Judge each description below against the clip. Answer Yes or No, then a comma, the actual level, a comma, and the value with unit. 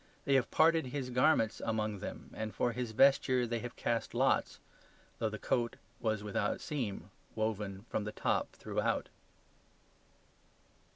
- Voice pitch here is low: Yes, low, 115 Hz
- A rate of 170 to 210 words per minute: No, average, 140 wpm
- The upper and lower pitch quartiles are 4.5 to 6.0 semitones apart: No, average, 2.8 semitones